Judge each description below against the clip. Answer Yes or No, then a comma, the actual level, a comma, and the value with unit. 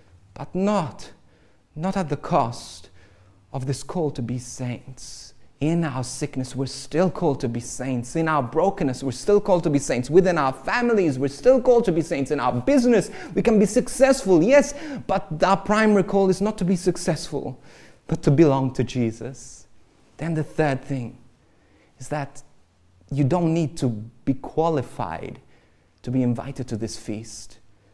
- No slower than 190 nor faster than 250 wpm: No, average, 170 wpm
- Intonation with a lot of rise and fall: Yes, wide, 6.8 semitones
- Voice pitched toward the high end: No, medium, 140 Hz